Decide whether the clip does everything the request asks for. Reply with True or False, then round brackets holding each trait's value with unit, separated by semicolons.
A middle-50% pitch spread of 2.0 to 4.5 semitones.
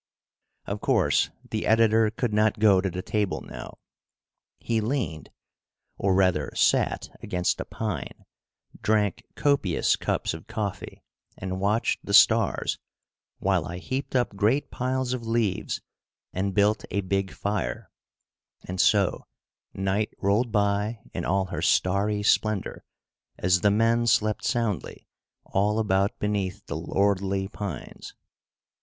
True (2.5 semitones)